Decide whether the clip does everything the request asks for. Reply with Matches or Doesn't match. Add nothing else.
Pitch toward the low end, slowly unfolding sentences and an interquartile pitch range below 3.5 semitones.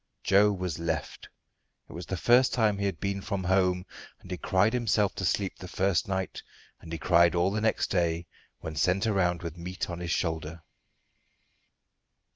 Doesn't match